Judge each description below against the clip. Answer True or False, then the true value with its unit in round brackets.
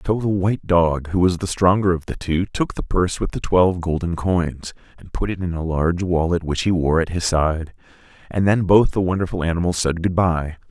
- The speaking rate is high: True (230 wpm)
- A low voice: True (90 Hz)